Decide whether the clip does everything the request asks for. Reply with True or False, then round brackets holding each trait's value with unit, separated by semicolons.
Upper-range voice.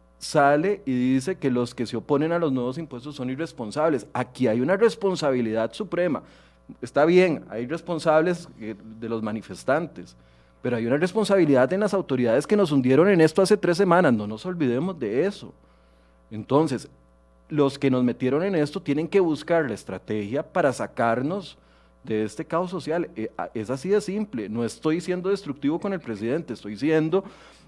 False (140 Hz)